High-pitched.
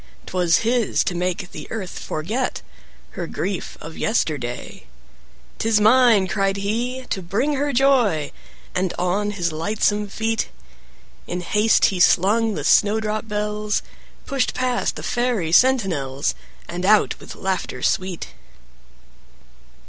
Yes: high, 205 Hz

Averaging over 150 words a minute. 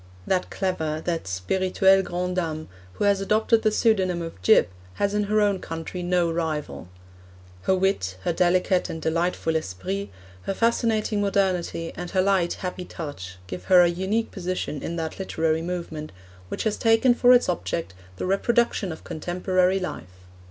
Yes: average, 160 wpm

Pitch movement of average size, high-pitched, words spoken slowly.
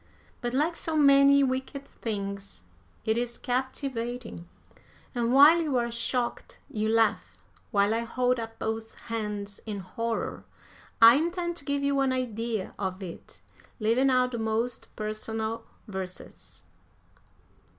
Yes: average, 3.3 semitones; high, 235 Hz; slow, 130 wpm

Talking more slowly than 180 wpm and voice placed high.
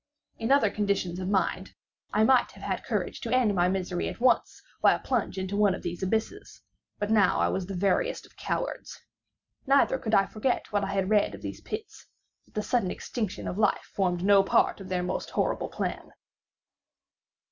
No: average, 190 wpm; high, 205 Hz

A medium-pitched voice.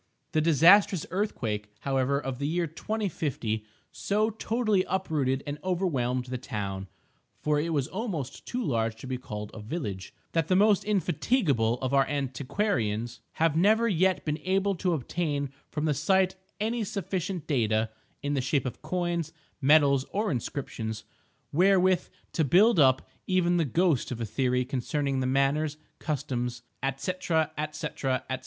Yes: medium, 150 Hz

